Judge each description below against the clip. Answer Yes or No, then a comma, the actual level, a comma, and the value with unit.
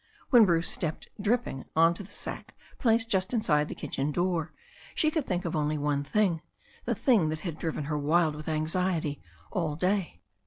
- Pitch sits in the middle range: Yes, medium, 165 Hz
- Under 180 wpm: No, average, 185 wpm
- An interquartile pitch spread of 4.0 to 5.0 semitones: Yes, average, 4.3 semitones